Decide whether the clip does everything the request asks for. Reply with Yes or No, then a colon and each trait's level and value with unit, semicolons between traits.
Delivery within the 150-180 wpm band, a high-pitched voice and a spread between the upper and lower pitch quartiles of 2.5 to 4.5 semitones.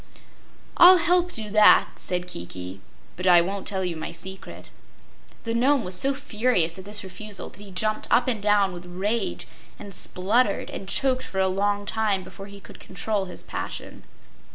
Yes: average, 175 wpm; high, 200 Hz; average, 3.3 semitones